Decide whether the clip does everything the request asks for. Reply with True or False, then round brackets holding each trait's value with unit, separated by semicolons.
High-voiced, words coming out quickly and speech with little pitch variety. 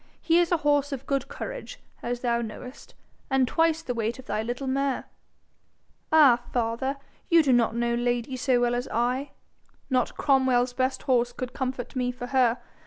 False (255 Hz; 175 wpm; 2.3 semitones)